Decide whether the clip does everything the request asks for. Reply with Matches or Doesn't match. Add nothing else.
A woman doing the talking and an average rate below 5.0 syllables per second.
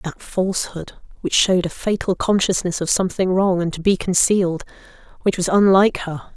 Doesn't match